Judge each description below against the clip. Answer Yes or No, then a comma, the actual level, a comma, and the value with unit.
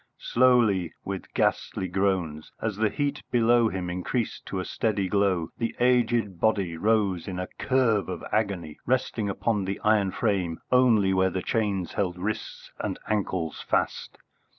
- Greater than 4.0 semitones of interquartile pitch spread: No, average, 3.5 semitones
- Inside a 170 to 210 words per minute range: No, average, 150 wpm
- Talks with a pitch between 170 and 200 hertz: No, low, 100 Hz